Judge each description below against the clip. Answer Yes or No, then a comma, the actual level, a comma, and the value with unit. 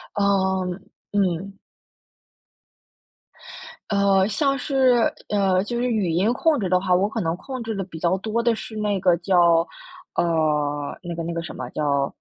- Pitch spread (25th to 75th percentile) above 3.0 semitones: Yes, average, 4.2 semitones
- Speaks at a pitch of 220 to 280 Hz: No, high, 190 Hz